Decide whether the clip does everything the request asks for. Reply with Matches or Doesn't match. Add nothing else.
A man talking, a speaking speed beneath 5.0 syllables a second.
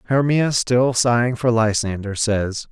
Matches